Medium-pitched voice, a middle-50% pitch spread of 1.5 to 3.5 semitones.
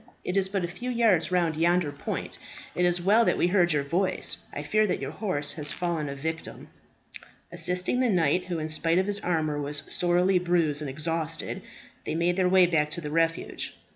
Yes: medium, 175 Hz; average, 2.7 semitones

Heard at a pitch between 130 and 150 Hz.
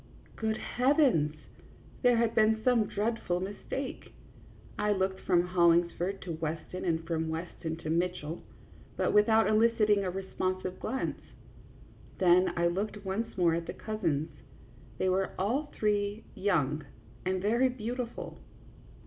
No: high, 190 Hz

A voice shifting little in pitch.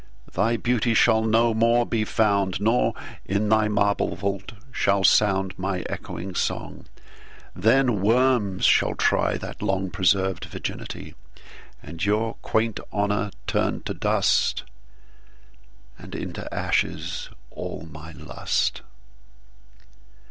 No: average, 3.2 semitones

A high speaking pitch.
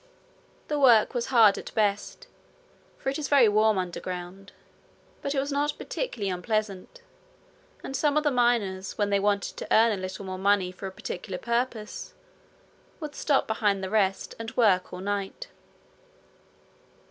Yes: high, 210 Hz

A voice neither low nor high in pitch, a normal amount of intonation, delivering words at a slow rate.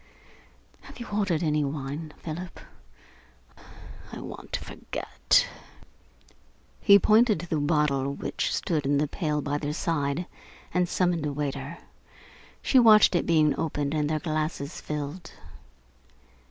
Yes: medium, 155 Hz; average, 3.2 semitones; slow, 130 wpm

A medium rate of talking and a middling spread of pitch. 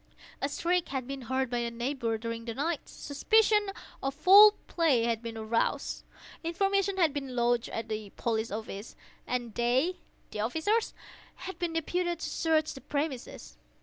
No: average, 160 wpm; wide, 6.5 semitones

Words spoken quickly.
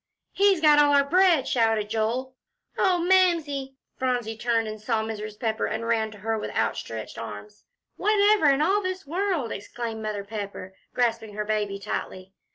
No: average, 165 wpm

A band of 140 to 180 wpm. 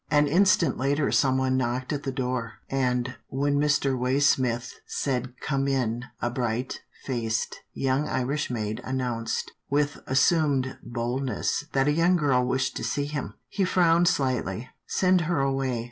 Yes: average, 160 wpm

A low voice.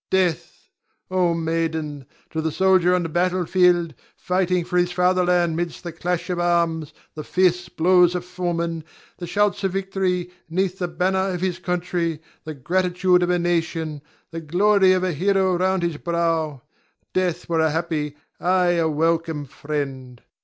No: medium, 175 Hz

